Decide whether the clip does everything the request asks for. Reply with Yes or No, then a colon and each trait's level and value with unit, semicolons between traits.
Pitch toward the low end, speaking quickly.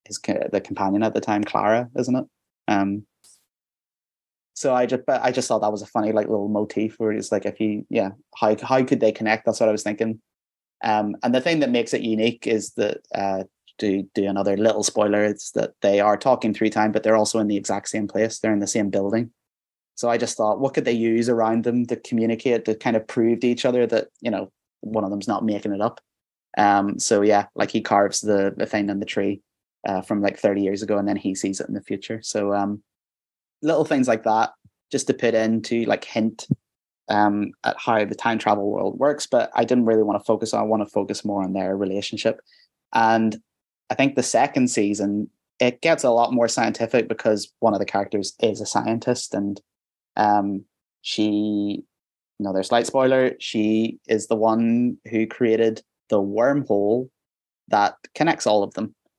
Yes: low, 110 Hz; fast, 210 wpm